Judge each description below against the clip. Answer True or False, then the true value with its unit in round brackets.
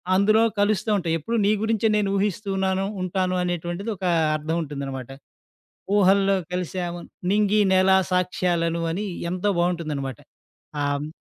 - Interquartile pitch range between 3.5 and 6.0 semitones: False (3.1 semitones)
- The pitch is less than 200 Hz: True (185 Hz)